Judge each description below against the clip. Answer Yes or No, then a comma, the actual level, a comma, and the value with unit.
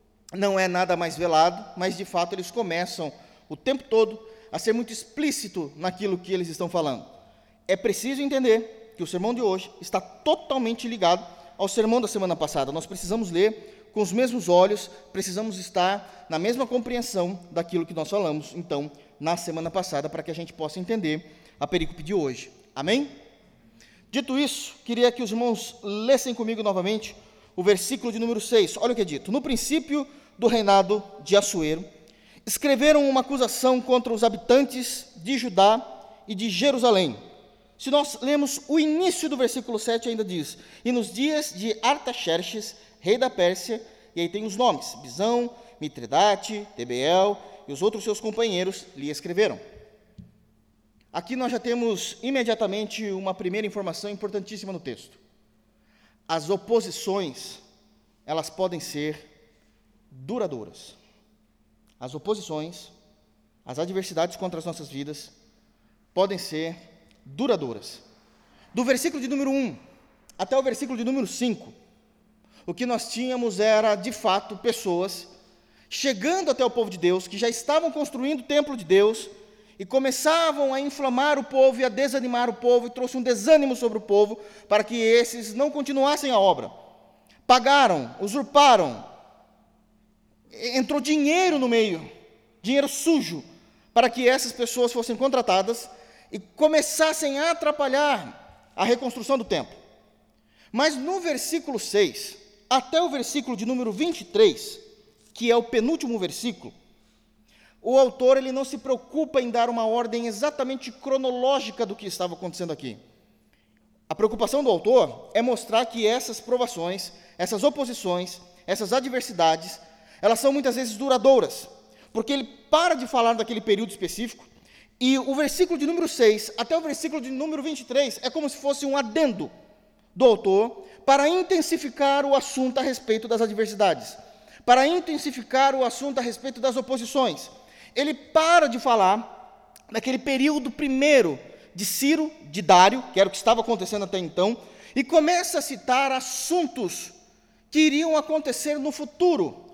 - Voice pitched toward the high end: Yes, high, 230 Hz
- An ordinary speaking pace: Yes, average, 150 wpm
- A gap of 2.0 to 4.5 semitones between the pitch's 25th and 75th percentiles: No, wide, 5.5 semitones